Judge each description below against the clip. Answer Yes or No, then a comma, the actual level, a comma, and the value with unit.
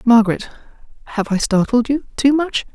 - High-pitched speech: Yes, high, 245 Hz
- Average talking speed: Yes, average, 155 wpm